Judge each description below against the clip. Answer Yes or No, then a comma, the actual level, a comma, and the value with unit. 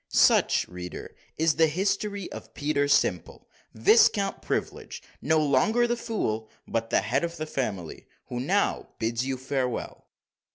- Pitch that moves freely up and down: Yes, wide, 8.0 semitones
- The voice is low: No, medium, 145 Hz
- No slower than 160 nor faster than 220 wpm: No, average, 140 wpm